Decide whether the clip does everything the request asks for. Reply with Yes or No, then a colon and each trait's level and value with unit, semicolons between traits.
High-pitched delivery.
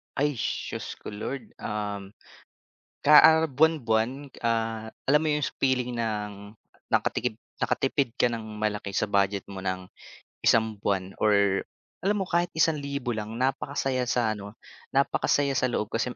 No: low, 115 Hz